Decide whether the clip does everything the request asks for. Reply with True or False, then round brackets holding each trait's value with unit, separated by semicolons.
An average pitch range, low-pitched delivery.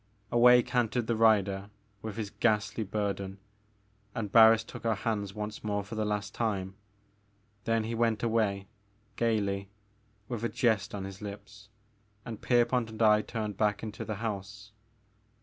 False (2.0 semitones; 110 Hz)